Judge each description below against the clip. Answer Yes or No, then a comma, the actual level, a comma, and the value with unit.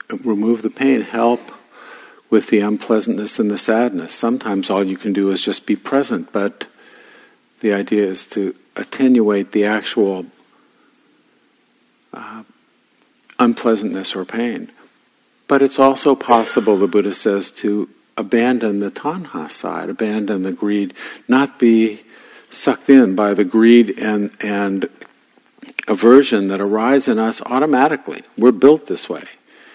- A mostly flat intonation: No, average, 3.0 semitones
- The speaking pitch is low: Yes, low, 110 Hz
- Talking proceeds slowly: Yes, slow, 130 wpm